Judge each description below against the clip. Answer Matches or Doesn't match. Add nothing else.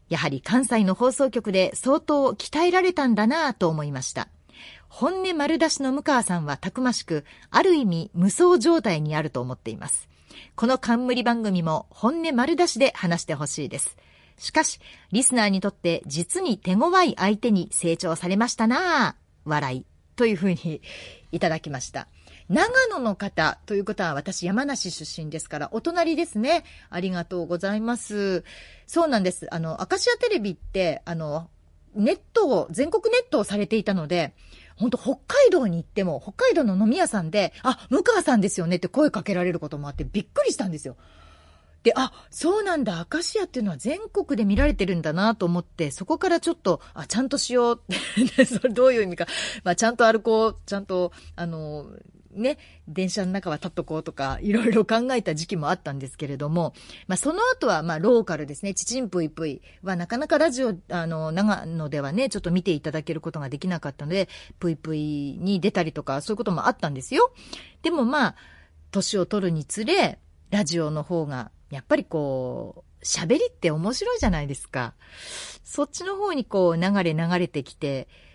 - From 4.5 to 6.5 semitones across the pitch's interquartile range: Doesn't match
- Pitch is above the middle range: Matches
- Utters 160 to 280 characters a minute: Doesn't match